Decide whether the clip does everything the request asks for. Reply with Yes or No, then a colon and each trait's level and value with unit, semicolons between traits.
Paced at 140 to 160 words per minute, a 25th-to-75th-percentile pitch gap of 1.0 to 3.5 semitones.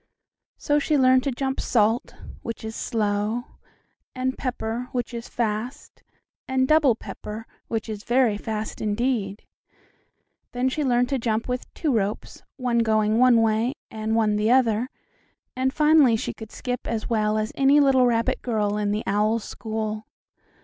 Yes: average, 155 wpm; average, 2.9 semitones